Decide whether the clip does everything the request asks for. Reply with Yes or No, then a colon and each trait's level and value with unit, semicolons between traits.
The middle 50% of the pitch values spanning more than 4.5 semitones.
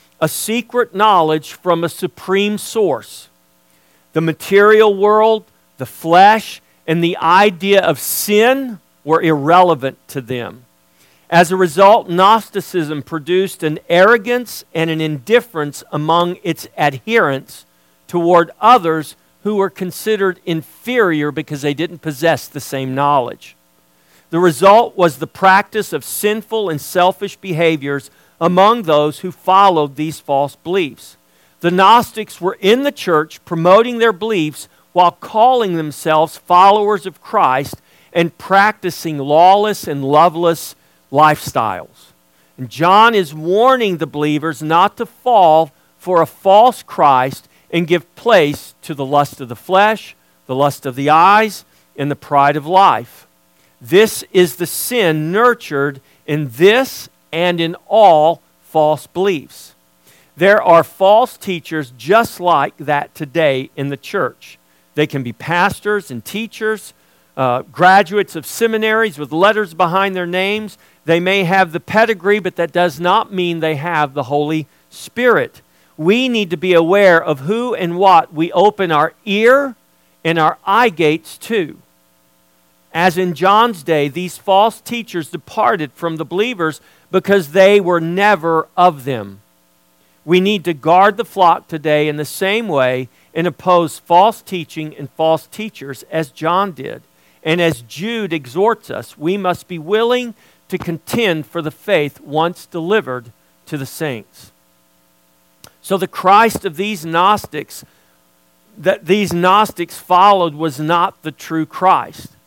Yes: average, 5.2 semitones